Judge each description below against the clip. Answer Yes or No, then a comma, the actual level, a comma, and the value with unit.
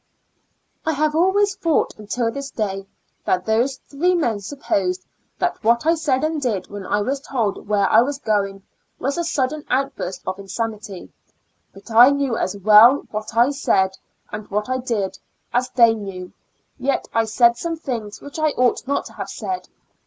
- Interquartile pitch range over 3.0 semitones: Yes, wide, 5.4 semitones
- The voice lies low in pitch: No, high, 235 Hz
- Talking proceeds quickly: No, average, 175 wpm